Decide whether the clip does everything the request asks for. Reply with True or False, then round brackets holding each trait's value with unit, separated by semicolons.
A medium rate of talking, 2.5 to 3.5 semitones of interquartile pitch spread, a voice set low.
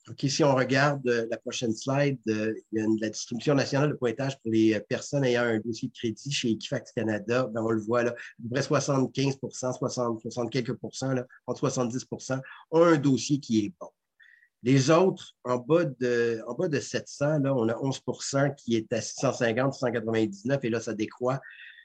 True (200 wpm; 3.0 semitones; 125 Hz)